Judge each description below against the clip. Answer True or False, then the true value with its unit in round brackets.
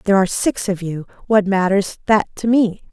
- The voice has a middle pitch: False (200 Hz)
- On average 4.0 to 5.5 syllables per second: True (5.4 syllables/s)